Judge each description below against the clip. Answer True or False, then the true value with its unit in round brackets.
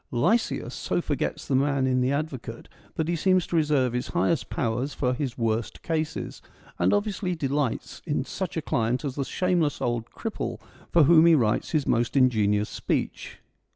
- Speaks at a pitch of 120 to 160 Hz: True (140 Hz)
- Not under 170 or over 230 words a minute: True (175 wpm)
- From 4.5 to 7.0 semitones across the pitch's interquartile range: True (5.0 semitones)